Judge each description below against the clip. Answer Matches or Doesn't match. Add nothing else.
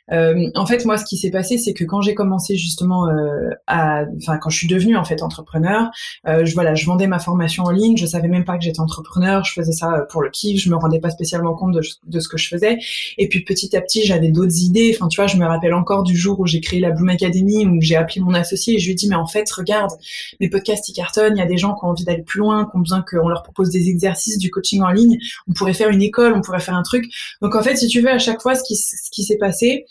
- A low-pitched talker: Doesn't match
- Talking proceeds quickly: Matches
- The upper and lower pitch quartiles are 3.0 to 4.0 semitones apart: Matches